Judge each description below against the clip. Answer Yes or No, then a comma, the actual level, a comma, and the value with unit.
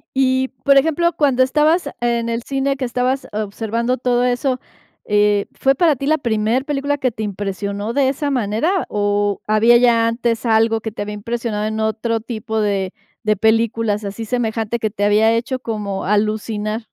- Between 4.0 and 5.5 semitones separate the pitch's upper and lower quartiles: No, average, 3.3 semitones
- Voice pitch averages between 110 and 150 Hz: No, high, 230 Hz